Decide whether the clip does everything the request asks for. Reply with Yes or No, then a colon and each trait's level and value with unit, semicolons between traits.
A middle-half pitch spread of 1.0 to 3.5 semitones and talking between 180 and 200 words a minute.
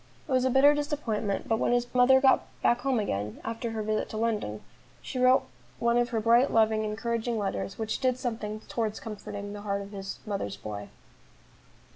Yes: average, 3.1 semitones; average, 190 wpm